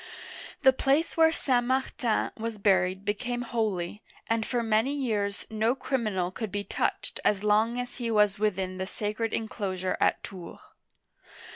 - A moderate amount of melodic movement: Yes, average, 3.4 semitones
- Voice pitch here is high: Yes, high, 215 Hz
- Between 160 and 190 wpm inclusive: No, average, 150 wpm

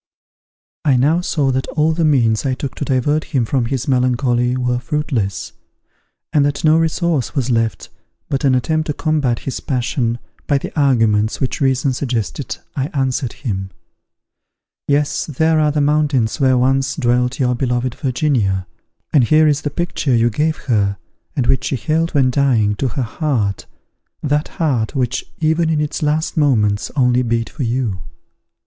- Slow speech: No, average, 165 wpm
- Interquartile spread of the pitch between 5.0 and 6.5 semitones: No, average, 3.6 semitones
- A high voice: No, low, 135 Hz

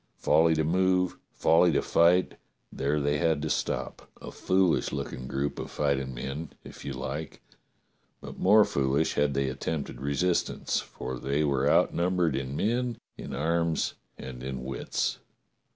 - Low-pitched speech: Yes, very low, 75 Hz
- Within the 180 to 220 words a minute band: No, average, 150 wpm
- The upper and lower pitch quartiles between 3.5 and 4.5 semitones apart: Yes, average, 4.0 semitones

